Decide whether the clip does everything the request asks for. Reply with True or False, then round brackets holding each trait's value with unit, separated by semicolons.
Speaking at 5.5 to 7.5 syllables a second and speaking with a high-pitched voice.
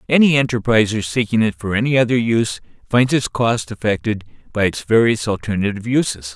False (5.8 syllables/s; 110 Hz)